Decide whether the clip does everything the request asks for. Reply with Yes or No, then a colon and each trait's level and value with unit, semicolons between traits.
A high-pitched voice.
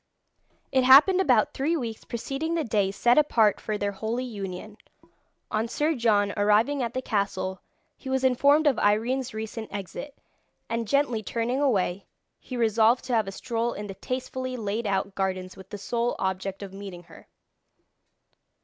Yes: high, 225 Hz